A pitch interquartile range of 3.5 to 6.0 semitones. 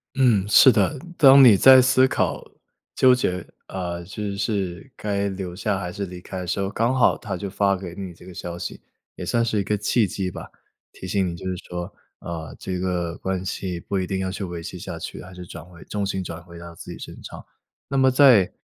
No: average, 3.0 semitones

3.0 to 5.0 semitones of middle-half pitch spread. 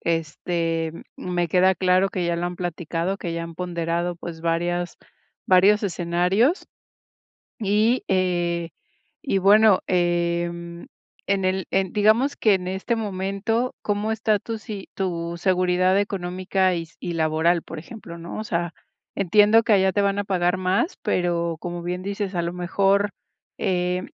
No: narrow, 2.5 semitones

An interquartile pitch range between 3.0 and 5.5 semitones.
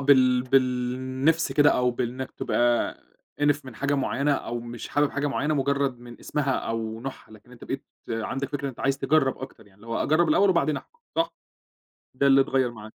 No: narrow, 2.6 semitones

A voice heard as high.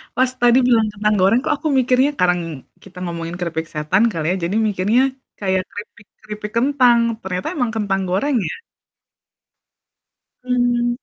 Yes: high, 210 Hz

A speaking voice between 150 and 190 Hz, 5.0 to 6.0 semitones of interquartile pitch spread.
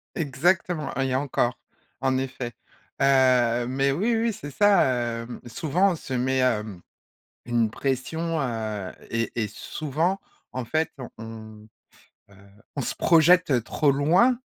No: low, 135 Hz; average, 5.3 semitones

